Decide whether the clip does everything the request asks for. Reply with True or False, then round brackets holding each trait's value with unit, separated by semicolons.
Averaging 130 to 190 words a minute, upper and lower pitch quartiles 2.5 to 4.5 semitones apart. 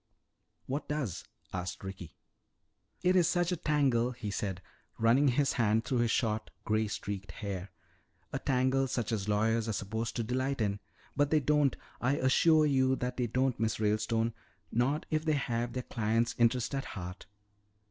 True (170 wpm; 4.0 semitones)